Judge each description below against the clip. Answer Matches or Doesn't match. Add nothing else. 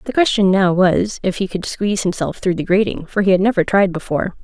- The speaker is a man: Doesn't match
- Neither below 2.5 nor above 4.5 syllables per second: Doesn't match